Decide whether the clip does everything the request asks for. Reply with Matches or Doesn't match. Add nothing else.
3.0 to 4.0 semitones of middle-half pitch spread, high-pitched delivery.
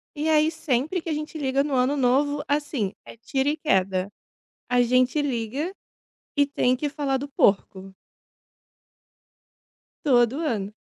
Matches